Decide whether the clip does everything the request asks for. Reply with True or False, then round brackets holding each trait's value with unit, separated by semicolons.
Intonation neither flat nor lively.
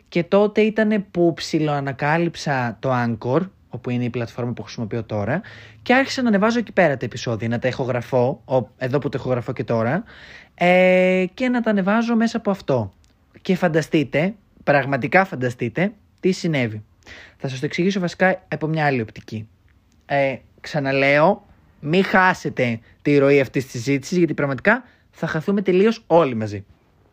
False (7.1 semitones)